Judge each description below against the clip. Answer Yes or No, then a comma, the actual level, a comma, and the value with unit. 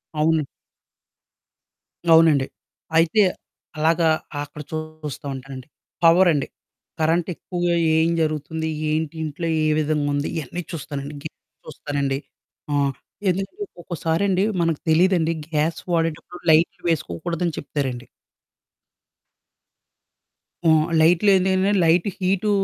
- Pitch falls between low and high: Yes, medium, 160 Hz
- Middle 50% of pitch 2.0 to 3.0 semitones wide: Yes, narrow, 2.5 semitones